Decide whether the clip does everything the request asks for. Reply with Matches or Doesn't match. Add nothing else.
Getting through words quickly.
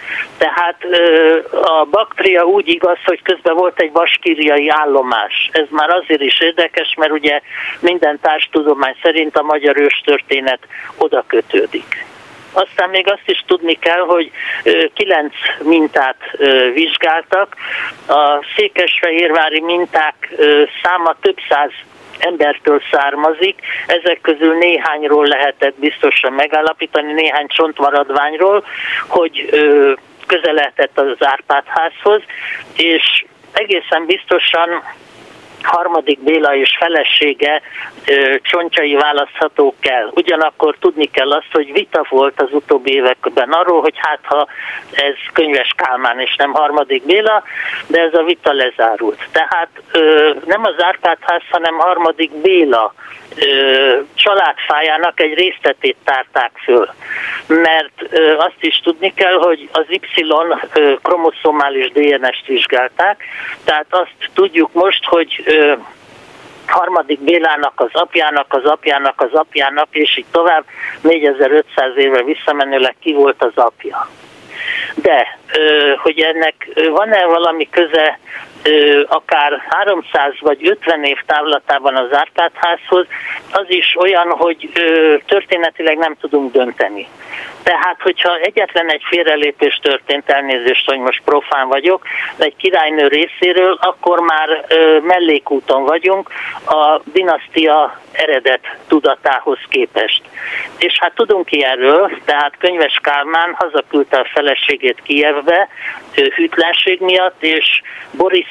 Doesn't match